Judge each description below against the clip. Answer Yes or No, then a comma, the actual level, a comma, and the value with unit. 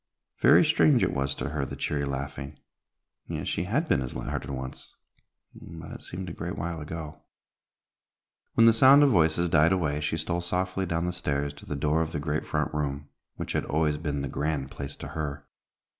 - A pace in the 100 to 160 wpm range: No, fast, 205 wpm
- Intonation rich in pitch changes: No, average, 3.3 semitones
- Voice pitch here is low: Yes, very low, 80 Hz